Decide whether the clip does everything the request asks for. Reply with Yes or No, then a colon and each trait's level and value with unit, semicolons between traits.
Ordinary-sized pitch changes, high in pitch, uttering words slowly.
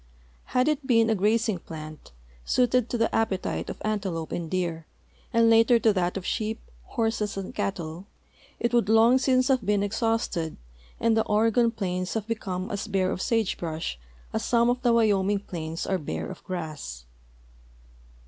No: average, 4.1 semitones; high, 210 Hz; average, 165 wpm